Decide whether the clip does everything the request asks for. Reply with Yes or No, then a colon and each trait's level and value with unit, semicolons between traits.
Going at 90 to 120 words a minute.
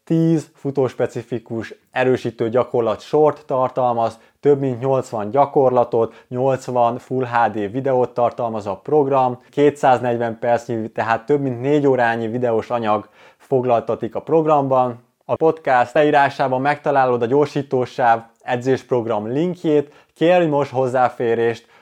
Yes: average, 110 wpm